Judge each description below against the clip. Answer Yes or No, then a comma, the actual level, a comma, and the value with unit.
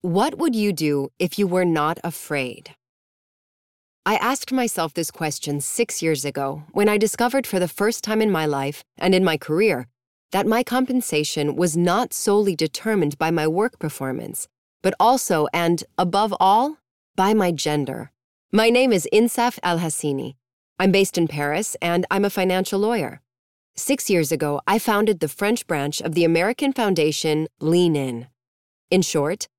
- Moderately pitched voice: Yes, medium, 175 Hz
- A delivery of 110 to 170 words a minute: Yes, average, 160 wpm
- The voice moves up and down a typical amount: No, wide, 5.7 semitones